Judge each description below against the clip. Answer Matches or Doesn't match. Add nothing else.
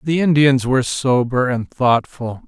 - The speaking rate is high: Doesn't match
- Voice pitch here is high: Doesn't match